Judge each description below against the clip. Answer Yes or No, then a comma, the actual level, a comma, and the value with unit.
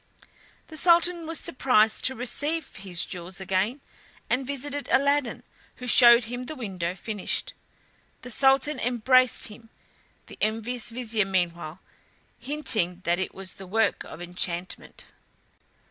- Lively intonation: Yes, wide, 5.9 semitones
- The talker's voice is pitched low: No, high, 235 Hz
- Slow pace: Yes, slow, 130 wpm